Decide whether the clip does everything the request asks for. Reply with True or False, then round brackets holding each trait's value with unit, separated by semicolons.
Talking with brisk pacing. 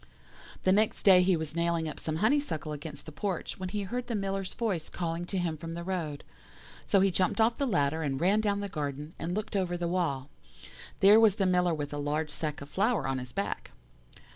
True (220 wpm)